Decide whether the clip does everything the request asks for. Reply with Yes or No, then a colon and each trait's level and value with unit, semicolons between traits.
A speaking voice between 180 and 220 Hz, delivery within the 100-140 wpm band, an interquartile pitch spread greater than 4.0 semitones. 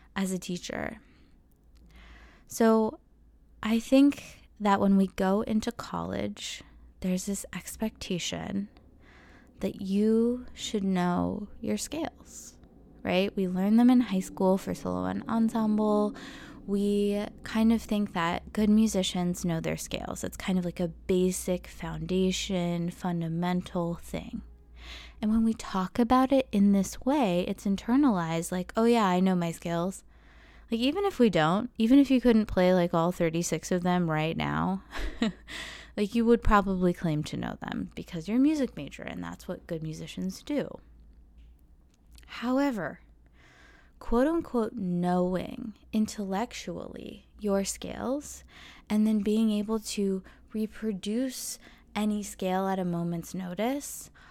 Yes: high, 190 Hz; slow, 135 wpm; average, 4.8 semitones